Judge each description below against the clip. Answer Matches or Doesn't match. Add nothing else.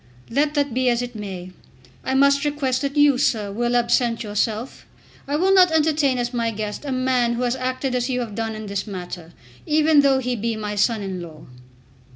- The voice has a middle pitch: Doesn't match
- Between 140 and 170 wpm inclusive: Doesn't match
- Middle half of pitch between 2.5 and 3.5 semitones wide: Doesn't match